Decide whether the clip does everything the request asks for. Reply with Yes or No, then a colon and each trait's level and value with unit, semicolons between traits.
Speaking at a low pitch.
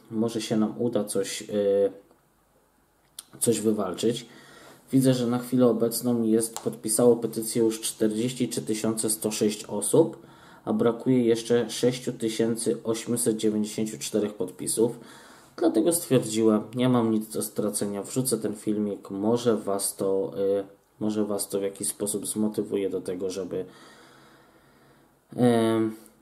Yes: low, 110 Hz